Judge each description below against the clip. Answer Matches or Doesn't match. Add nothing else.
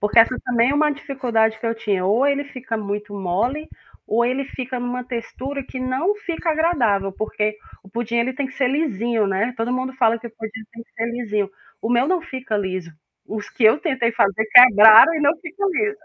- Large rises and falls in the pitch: Doesn't match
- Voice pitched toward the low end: Doesn't match